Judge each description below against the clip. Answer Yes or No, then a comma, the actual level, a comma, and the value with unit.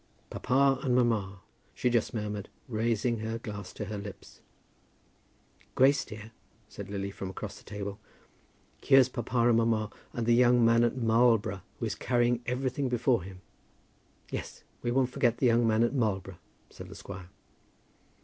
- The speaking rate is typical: Yes, average, 160 wpm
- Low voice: Yes, low, 115 Hz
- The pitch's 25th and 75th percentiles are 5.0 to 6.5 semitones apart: No, average, 3.0 semitones